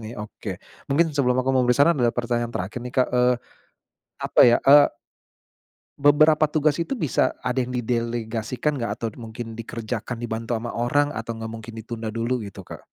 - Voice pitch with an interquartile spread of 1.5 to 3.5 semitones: Yes, average, 2.9 semitones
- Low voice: Yes, low, 120 Hz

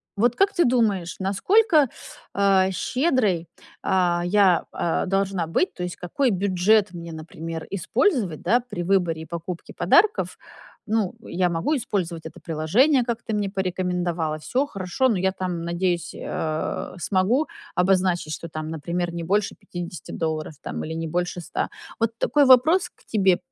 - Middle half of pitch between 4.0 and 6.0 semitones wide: Yes, average, 4.6 semitones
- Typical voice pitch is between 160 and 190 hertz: Yes, medium, 185 Hz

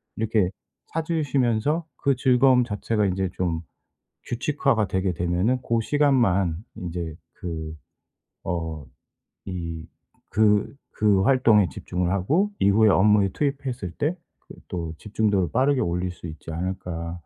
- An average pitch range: No, wide, 6.2 semitones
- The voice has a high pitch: No, low, 100 Hz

